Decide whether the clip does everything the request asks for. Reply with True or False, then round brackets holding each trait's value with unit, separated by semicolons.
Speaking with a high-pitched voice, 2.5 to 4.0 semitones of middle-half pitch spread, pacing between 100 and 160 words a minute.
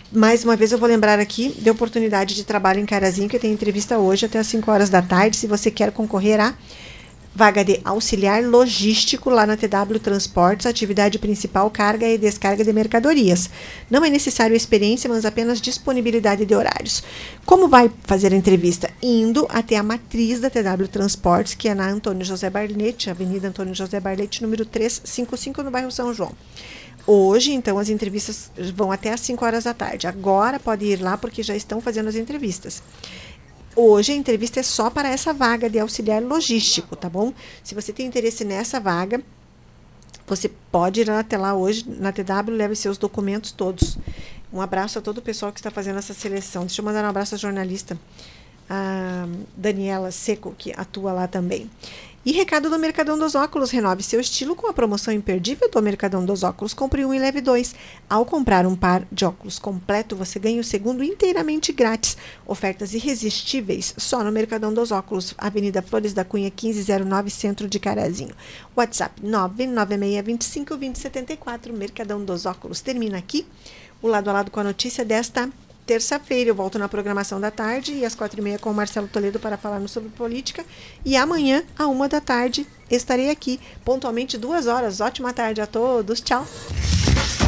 False (215 Hz; 3.2 semitones; 180 wpm)